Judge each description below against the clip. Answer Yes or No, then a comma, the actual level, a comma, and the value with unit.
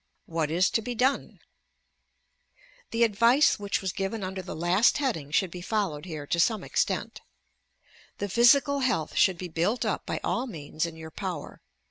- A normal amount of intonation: No, wide, 5.7 semitones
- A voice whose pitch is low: No, high, 190 Hz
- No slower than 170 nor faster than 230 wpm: Yes, average, 175 wpm